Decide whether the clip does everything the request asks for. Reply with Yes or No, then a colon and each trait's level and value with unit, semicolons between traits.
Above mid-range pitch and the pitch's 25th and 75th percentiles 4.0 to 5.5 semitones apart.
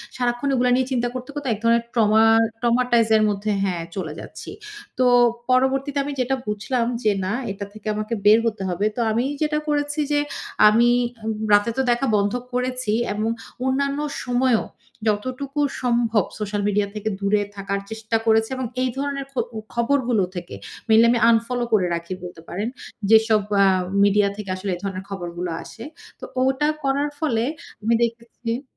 No: high, 230 Hz; average, 3.5 semitones